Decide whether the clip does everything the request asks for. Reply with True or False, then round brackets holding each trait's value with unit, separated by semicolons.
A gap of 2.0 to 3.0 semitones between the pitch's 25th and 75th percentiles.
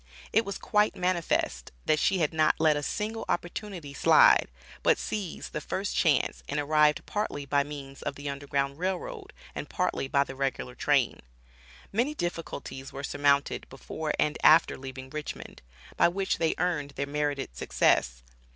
False (3.9 semitones)